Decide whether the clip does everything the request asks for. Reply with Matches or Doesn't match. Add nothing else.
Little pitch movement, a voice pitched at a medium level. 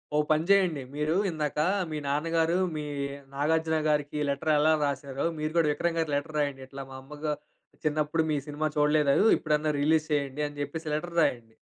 Matches